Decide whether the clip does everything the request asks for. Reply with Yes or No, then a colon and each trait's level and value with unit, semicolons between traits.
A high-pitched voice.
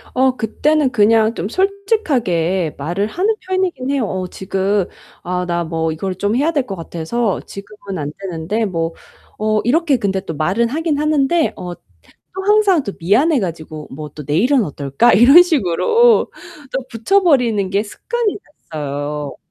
Yes: high, 215 Hz